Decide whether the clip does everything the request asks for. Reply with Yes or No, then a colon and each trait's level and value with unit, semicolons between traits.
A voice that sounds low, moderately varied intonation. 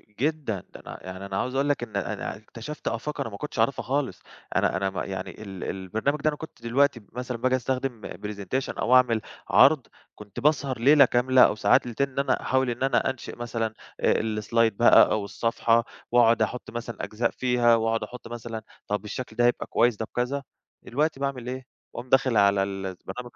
Yes: low, 120 Hz; average, 3.3 semitones